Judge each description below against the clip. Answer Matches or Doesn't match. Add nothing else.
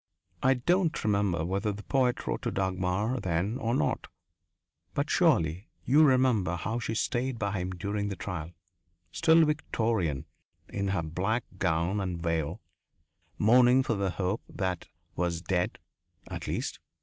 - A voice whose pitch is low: Matches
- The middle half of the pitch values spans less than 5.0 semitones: Doesn't match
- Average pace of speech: Matches